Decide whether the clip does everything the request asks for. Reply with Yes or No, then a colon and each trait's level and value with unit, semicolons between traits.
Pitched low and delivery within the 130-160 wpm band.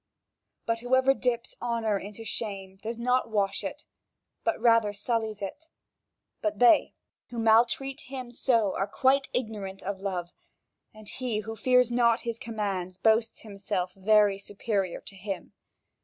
No: high, 220 Hz; average, 140 wpm